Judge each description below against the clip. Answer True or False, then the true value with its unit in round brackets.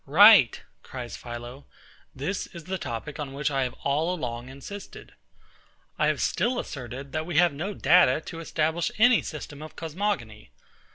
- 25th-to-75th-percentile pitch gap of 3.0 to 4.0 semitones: False (5.2 semitones)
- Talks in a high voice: False (150 Hz)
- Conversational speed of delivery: True (160 wpm)